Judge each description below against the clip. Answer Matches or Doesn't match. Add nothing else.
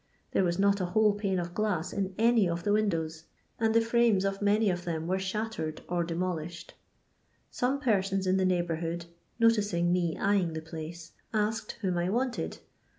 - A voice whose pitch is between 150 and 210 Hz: Matches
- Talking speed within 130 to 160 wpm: Doesn't match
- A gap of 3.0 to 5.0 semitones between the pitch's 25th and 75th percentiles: Matches